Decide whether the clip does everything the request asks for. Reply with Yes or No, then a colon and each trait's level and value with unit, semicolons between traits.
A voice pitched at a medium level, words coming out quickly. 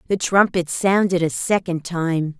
No: medium, 175 Hz; average, 150 wpm